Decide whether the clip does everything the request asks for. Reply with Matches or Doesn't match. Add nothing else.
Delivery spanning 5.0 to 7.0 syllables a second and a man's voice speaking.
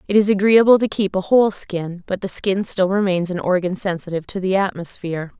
Doesn't match